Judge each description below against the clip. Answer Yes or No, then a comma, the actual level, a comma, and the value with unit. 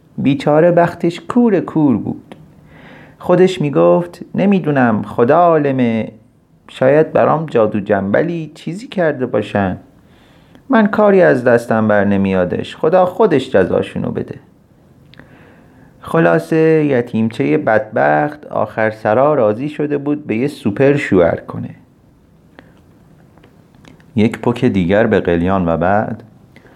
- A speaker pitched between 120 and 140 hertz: Yes, low, 135 Hz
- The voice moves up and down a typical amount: No, wide, 7.6 semitones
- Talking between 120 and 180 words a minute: No, slow, 105 wpm